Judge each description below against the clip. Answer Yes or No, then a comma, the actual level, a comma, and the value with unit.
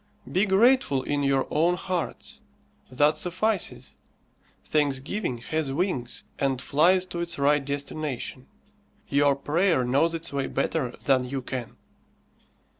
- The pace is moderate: No, slow, 120 wpm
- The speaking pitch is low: No, medium, 145 Hz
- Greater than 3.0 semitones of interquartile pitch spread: Yes, average, 4.2 semitones